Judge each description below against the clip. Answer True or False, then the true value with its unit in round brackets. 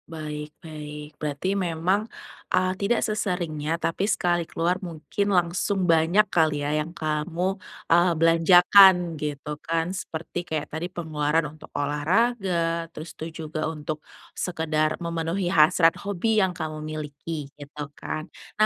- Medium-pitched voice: True (165 Hz)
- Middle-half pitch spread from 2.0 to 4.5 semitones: True (2.7 semitones)